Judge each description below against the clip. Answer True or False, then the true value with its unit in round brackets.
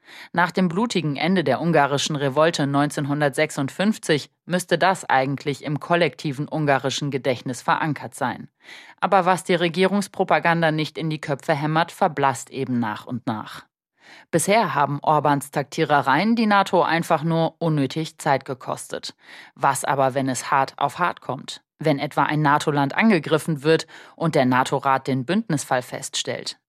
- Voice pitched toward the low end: False (155 Hz)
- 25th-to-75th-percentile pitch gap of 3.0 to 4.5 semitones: True (3.6 semitones)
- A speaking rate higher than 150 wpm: False (140 wpm)